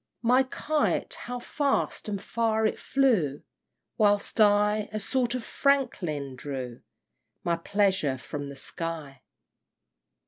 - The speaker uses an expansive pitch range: Yes, wide, 8.4 semitones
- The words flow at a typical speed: No, slow, 125 wpm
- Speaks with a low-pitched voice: No, high, 205 Hz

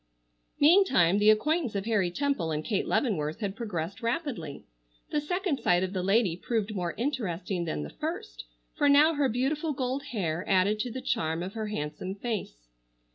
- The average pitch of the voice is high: Yes, high, 210 Hz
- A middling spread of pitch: No, wide, 7.2 semitones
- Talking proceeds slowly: No, average, 175 wpm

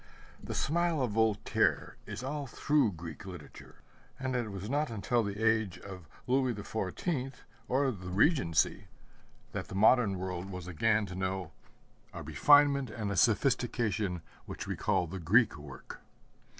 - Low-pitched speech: Yes, low, 110 Hz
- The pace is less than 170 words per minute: Yes, average, 145 wpm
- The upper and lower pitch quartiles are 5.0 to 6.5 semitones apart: Yes, wide, 5.6 semitones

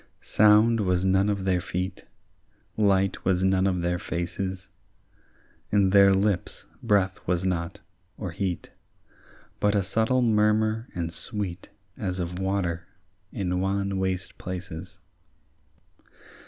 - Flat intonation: Yes, narrow, 1.9 semitones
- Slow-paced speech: Yes, slow, 120 wpm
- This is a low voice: Yes, very low, 95 Hz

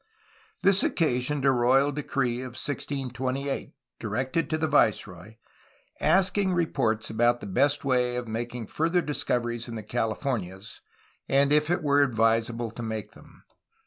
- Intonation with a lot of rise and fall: No, average, 4.0 semitones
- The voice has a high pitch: No, low, 125 Hz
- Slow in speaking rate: No, average, 145 wpm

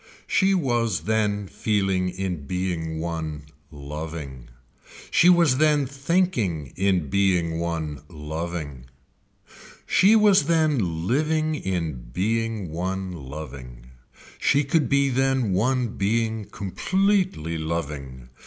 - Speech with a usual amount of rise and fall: No, wide, 8.8 semitones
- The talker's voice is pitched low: Yes, very low, 95 Hz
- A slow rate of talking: Yes, slow, 105 wpm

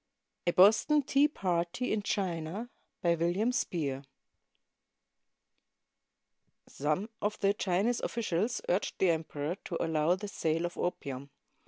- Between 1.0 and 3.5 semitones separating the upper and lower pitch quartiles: No, average, 4.3 semitones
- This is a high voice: No, medium, 180 Hz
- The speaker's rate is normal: No, slow, 120 wpm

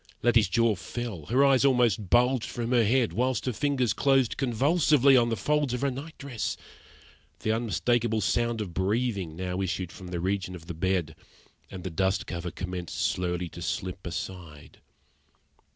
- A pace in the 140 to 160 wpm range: No, average, 170 wpm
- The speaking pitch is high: No, low, 110 Hz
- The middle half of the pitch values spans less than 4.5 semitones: No, wide, 5.4 semitones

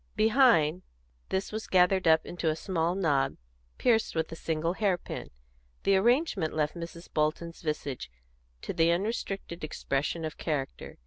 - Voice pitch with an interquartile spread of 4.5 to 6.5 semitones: No, average, 3.7 semitones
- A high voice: No, medium, 170 Hz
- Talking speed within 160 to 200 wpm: No, average, 145 wpm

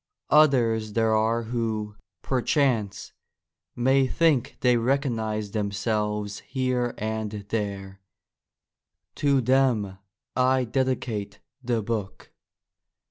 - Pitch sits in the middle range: No, low, 115 Hz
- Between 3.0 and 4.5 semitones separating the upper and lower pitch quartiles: Yes, average, 3.5 semitones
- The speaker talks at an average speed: No, slow, 85 wpm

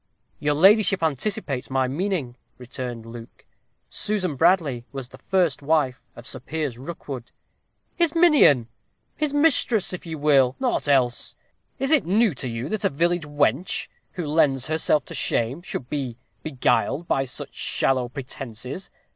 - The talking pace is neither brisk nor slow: Yes, average, 145 wpm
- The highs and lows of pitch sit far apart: Yes, wide, 6.0 semitones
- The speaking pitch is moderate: Yes, medium, 145 Hz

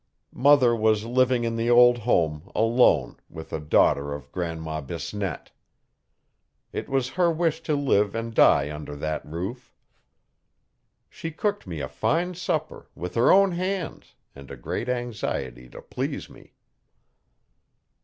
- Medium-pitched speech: No, low, 115 Hz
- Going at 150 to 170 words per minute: No, average, 140 wpm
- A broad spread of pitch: Yes, wide, 8.7 semitones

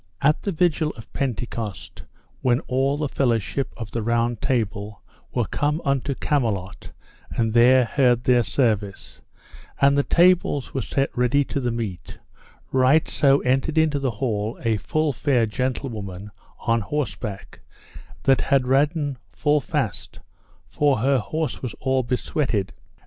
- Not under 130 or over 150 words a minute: Yes, average, 140 wpm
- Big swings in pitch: No, average, 3.7 semitones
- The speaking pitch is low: Yes, low, 130 Hz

